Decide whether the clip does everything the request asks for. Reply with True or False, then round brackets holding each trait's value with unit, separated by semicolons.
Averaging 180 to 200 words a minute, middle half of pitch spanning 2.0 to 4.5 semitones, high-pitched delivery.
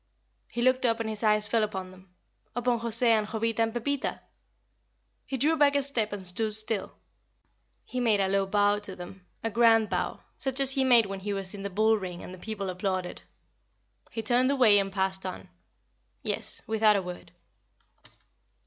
True (185 wpm; 3.4 semitones; 215 Hz)